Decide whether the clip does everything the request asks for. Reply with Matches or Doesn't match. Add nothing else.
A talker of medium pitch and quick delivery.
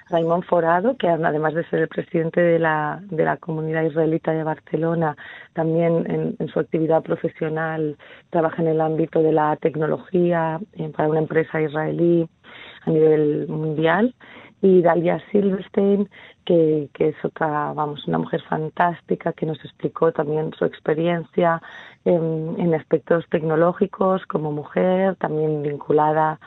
Doesn't match